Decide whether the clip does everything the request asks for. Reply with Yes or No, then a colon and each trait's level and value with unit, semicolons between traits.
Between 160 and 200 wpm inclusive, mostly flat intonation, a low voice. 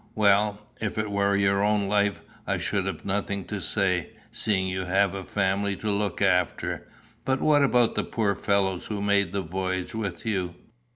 Yes: average, 180 wpm; narrow, 1.5 semitones; low, 100 Hz